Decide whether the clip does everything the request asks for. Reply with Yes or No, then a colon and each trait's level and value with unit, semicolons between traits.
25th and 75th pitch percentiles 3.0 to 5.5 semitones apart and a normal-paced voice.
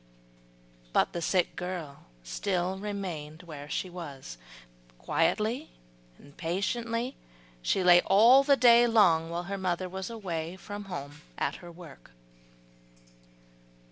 No: average, 3.8 semitones; slow, 120 wpm